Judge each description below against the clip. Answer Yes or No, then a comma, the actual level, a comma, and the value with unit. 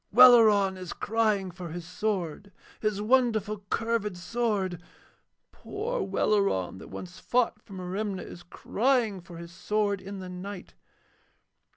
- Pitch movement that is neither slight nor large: Yes, average, 3.3 semitones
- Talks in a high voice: Yes, high, 200 Hz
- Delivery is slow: Yes, slow, 130 wpm